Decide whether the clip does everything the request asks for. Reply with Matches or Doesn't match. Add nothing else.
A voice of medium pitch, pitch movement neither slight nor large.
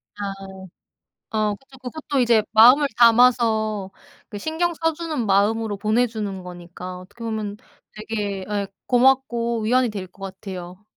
Doesn't match